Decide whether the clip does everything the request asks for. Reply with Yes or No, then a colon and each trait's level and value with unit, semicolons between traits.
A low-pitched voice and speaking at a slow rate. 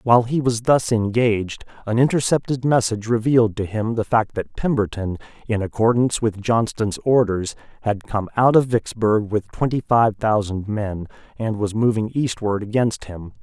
No: low, 110 Hz; average, 160 wpm